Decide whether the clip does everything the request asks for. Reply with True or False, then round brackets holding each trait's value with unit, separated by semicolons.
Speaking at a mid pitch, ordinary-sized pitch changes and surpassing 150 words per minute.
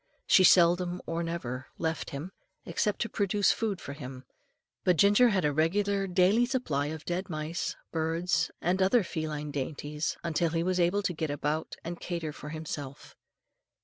True (170 Hz; 3.6 semitones; 165 wpm)